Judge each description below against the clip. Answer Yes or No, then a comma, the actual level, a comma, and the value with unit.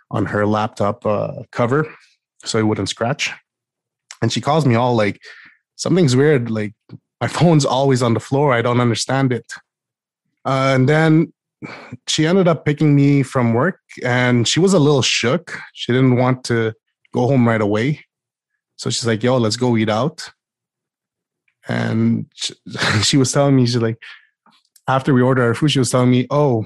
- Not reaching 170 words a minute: No, average, 175 wpm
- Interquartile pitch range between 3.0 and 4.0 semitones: Yes, average, 3.6 semitones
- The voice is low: Yes, low, 125 Hz